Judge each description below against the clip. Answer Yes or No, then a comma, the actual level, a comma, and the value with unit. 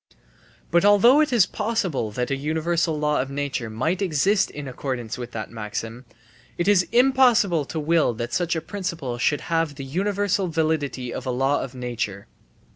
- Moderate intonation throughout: No, wide, 6.6 semitones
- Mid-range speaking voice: Yes, medium, 155 Hz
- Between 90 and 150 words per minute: No, average, 175 wpm